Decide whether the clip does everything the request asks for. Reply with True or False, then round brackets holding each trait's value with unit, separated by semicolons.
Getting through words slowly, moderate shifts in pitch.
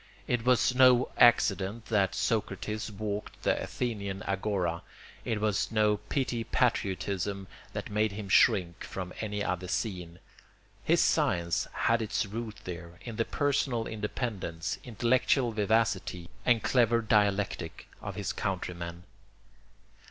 True (120 wpm; 3.4 semitones)